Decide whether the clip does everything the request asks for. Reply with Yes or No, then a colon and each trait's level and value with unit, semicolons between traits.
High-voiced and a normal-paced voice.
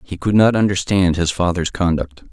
No: very low, 90 Hz; average, 180 wpm